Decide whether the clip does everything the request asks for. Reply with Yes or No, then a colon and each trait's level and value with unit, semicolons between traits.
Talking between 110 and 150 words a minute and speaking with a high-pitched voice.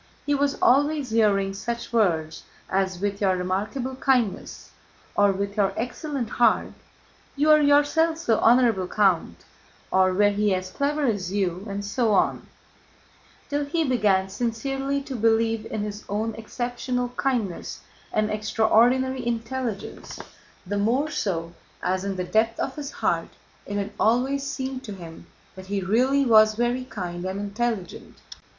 Yes: average, 145 wpm; high, 220 Hz